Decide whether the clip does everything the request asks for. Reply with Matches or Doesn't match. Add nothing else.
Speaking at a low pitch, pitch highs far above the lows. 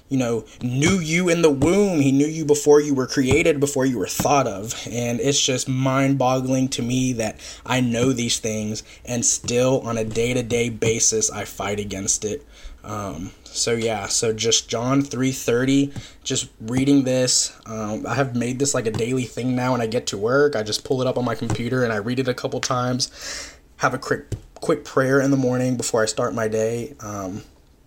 Doesn't match